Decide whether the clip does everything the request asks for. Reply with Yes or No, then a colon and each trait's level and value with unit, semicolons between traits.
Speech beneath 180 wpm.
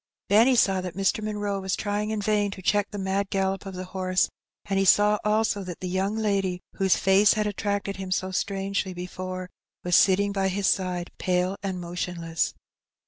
No: average, 190 wpm